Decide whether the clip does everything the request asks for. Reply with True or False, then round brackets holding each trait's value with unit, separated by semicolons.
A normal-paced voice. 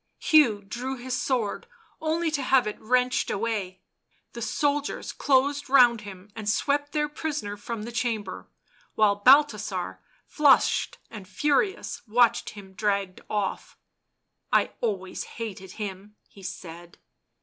False (130 wpm)